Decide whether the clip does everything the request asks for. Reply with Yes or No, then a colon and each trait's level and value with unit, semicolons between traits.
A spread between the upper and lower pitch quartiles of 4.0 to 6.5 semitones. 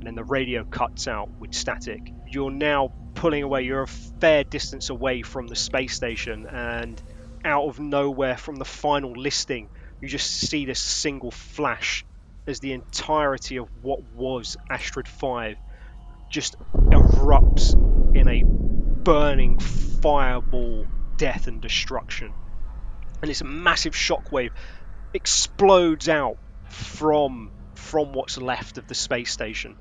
Yes: average, 4.5 semitones